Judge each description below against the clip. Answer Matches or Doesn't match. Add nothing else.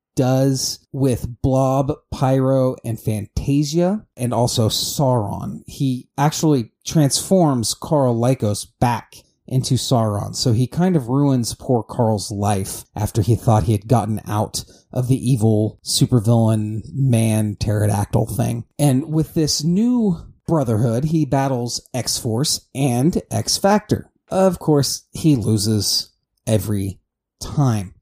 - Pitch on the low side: Matches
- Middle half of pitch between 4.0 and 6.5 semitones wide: Matches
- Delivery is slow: Matches